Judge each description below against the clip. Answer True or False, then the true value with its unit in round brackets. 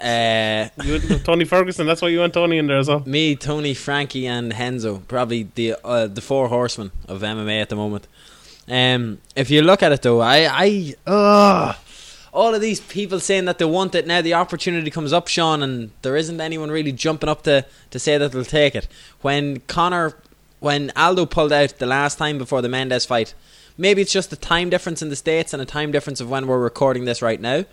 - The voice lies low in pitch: False (145 Hz)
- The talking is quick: True (215 wpm)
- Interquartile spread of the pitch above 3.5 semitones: True (5.2 semitones)